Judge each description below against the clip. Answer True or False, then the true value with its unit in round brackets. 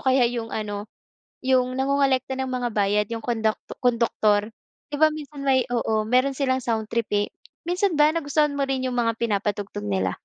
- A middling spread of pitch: True (3.8 semitones)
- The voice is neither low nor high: False (245 Hz)